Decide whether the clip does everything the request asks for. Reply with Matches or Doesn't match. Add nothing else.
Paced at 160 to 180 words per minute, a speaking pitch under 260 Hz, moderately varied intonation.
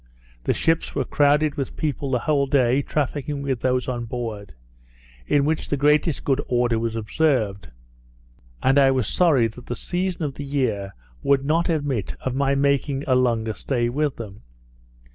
Matches